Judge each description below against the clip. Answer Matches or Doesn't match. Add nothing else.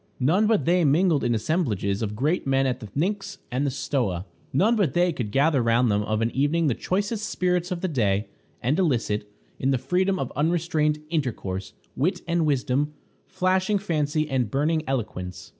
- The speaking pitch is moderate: Matches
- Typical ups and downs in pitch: Doesn't match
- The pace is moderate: Matches